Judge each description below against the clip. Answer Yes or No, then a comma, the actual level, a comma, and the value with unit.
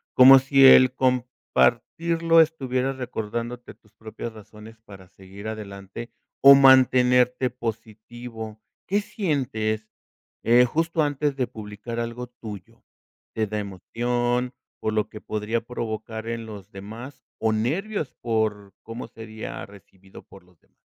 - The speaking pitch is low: Yes, low, 115 Hz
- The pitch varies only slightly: No, average, 3.0 semitones